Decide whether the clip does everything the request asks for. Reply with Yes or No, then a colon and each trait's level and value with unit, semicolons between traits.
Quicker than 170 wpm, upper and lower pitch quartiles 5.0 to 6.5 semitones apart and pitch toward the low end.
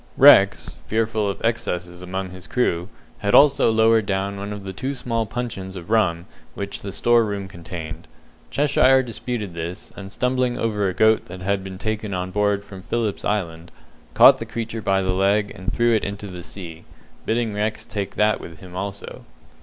No: average, 185 wpm; average, 3.2 semitones; low, 100 Hz